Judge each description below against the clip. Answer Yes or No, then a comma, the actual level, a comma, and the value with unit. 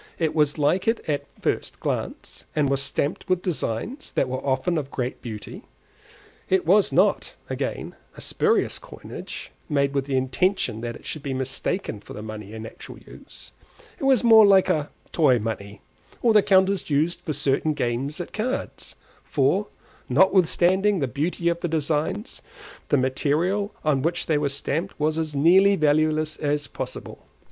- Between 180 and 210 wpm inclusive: No, average, 170 wpm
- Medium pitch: Yes, medium, 155 Hz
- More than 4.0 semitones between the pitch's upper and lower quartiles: Yes, average, 5.2 semitones